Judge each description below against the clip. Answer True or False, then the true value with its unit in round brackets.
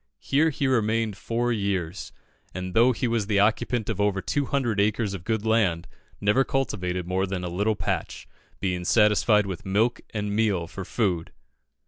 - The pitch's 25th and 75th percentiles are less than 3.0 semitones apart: False (3.4 semitones)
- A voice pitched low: True (105 Hz)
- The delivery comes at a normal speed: True (165 wpm)